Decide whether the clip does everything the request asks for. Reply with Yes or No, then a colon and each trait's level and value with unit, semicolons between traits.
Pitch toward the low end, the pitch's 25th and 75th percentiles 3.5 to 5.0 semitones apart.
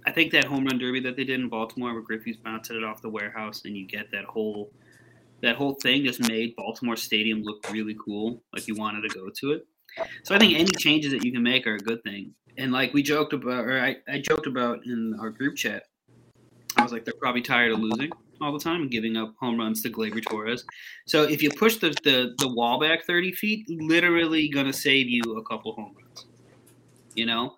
Yes: low, 125 Hz; average, 4.4 semitones